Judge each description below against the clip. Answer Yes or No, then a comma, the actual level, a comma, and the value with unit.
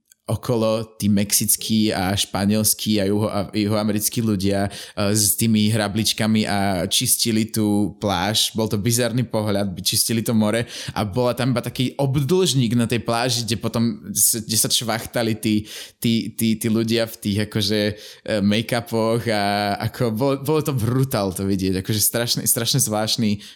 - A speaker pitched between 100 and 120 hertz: Yes, low, 110 Hz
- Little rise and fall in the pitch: Yes, narrow, 2.1 semitones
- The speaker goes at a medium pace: Yes, average, 150 wpm